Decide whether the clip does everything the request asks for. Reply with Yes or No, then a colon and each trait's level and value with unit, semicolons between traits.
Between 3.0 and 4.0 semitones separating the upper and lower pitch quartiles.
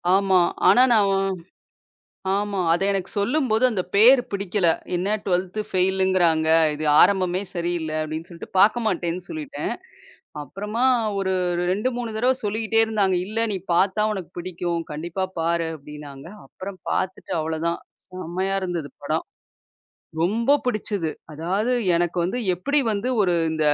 Yes: average, 3.7 semitones